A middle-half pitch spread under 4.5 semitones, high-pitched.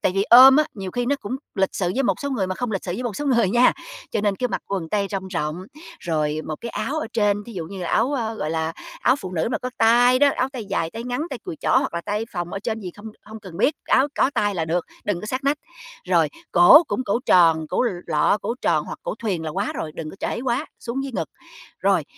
No: wide, 5.6 semitones; high, 210 Hz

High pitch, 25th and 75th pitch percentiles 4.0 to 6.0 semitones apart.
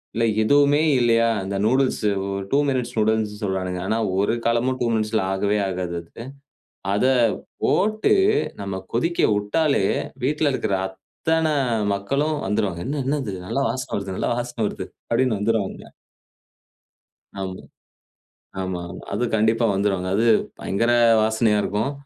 No: low, 110 Hz; average, 4.6 semitones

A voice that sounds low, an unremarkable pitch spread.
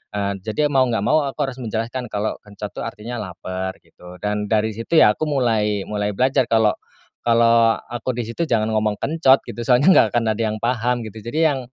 Yes: low, 115 Hz; average, 3.1 semitones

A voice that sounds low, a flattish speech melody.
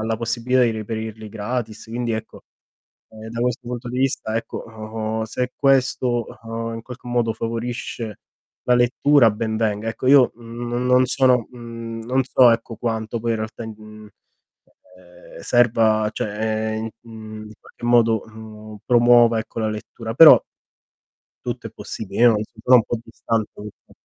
Yes: low, 115 Hz; narrow, 1.7 semitones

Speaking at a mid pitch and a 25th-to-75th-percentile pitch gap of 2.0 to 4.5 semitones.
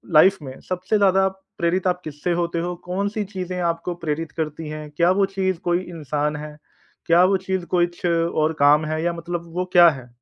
Yes: medium, 170 Hz; average, 2.8 semitones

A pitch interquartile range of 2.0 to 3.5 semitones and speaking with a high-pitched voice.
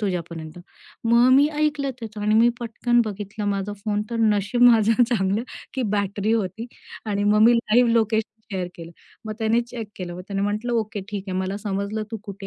Yes: narrow, 2.6 semitones; high, 215 Hz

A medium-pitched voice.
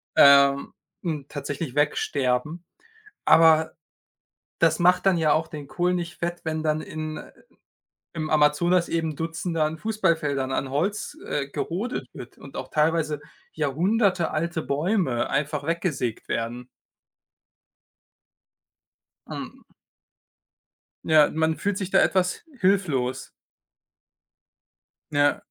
Yes: medium, 155 Hz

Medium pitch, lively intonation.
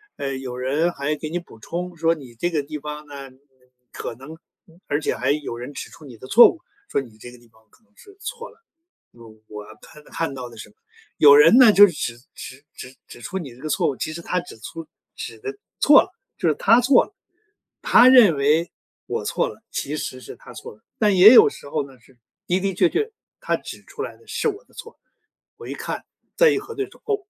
Yes: medium, 155 Hz; wide, 8.6 semitones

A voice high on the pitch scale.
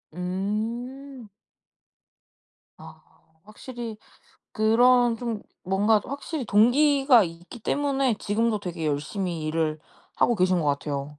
Yes: high, 215 Hz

